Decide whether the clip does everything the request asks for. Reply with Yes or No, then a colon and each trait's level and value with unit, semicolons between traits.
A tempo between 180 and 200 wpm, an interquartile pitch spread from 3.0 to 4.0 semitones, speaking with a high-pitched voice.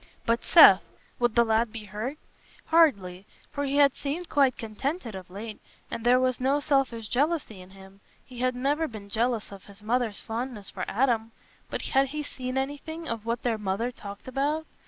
No: average, 185 wpm; average, 4.4 semitones; high, 240 Hz